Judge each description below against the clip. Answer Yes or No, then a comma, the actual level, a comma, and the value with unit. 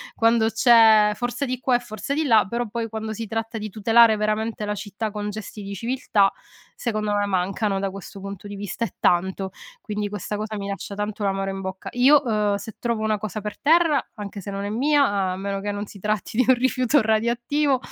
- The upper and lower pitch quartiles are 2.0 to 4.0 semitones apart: Yes, narrow, 2.6 semitones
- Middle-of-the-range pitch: No, high, 215 Hz